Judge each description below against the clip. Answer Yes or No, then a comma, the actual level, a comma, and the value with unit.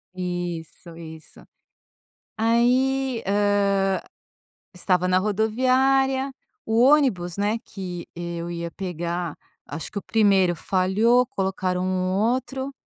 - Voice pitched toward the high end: Yes, high, 195 Hz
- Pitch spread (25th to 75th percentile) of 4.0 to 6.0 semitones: Yes, average, 5.0 semitones